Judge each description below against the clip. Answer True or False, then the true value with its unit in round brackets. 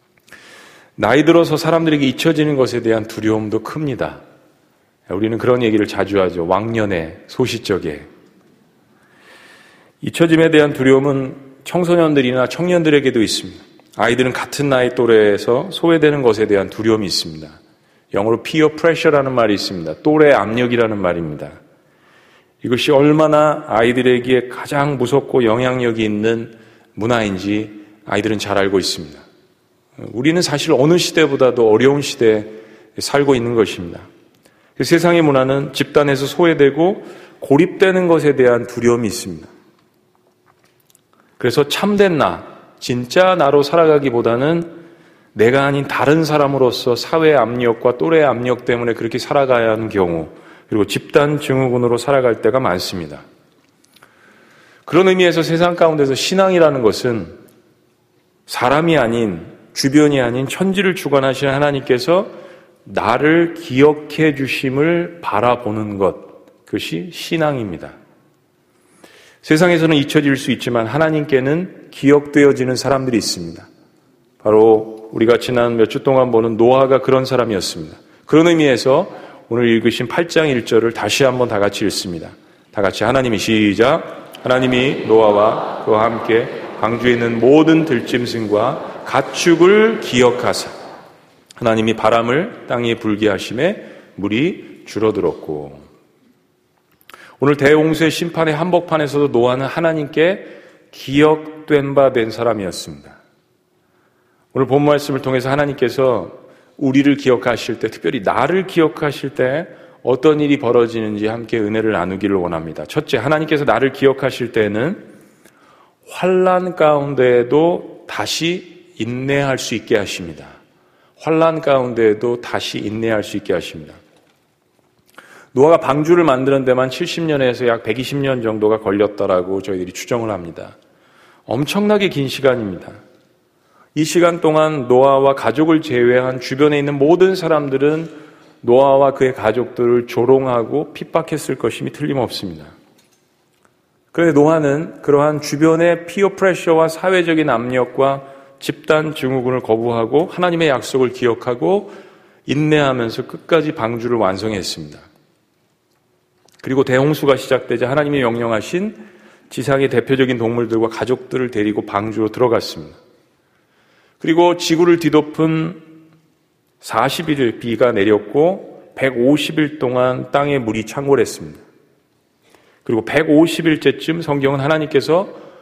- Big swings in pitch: False (5.0 semitones)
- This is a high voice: False (135 Hz)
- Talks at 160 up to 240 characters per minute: False (305 characters per minute)